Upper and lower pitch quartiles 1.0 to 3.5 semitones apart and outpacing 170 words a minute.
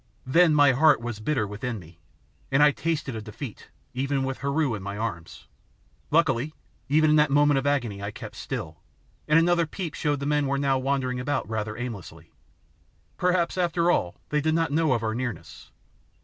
No: average, 4.7 semitones; average, 185 wpm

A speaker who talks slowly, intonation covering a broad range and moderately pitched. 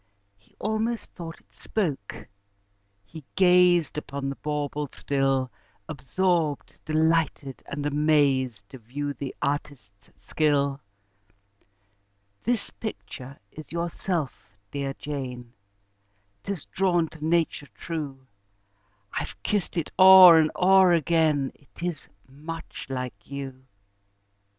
No: slow, 105 wpm; average, 3.9 semitones; medium, 150 Hz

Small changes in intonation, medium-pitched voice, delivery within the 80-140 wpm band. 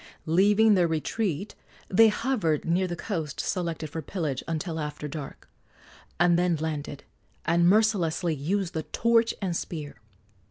No: average, 4.0 semitones; medium, 170 Hz; slow, 135 wpm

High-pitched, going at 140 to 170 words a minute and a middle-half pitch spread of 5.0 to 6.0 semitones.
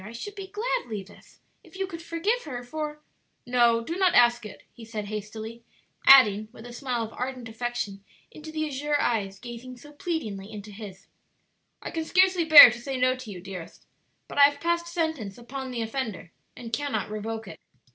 No: high, 245 Hz; average, 195 wpm; wide, 5.6 semitones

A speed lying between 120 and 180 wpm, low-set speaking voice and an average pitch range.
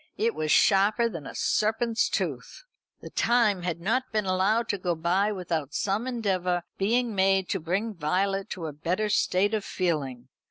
No: average, 170 wpm; high, 195 Hz; average, 3.7 semitones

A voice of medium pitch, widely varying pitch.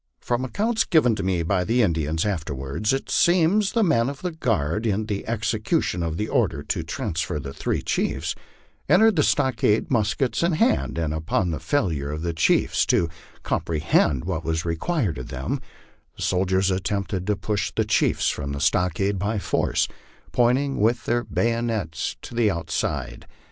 No: low, 100 Hz; wide, 6.9 semitones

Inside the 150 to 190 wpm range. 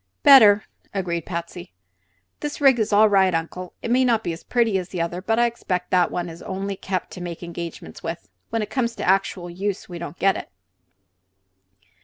No: average, 200 wpm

